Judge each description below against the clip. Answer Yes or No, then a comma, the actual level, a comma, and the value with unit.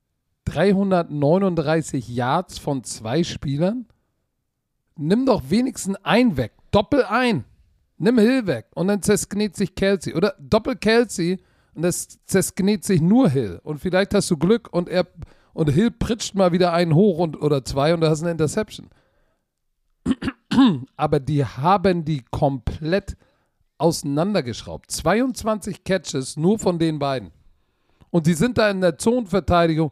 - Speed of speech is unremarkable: Yes, average, 140 wpm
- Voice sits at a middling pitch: Yes, medium, 175 Hz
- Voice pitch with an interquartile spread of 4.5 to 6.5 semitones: Yes, wide, 5.6 semitones